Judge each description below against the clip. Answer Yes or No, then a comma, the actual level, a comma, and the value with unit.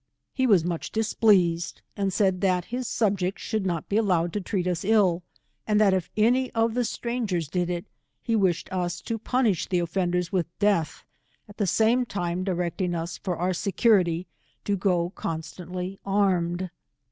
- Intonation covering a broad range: No, average, 3.3 semitones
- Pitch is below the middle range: No, medium, 185 Hz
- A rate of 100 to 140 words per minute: No, average, 170 wpm